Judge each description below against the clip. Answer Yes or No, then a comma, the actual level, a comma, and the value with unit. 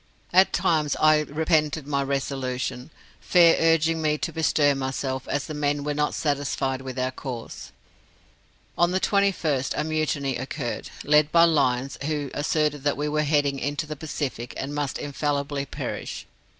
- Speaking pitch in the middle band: Yes, medium, 145 Hz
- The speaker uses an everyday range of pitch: No, narrow, 2.1 semitones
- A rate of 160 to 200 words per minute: No, average, 150 wpm